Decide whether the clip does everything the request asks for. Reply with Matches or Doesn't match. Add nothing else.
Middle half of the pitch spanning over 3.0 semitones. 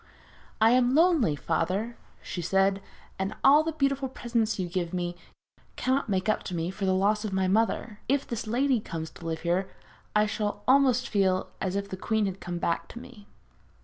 Matches